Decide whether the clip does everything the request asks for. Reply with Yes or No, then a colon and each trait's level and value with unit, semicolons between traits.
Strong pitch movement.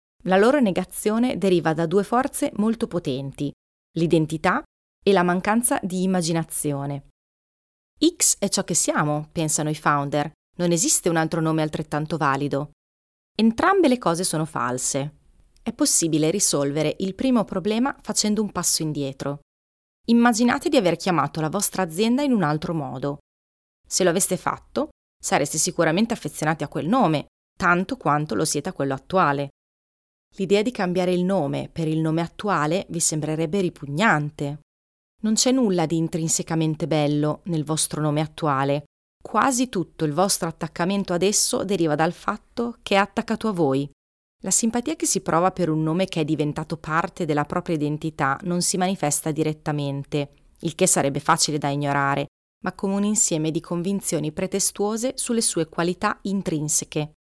No: average, 4.8 semitones